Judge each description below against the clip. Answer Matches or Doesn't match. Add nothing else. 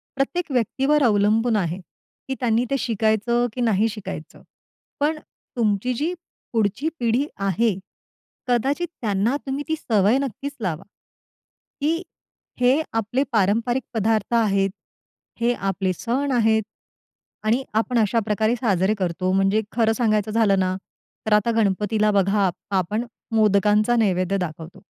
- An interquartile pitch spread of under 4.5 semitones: Matches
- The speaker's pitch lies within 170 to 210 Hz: Doesn't match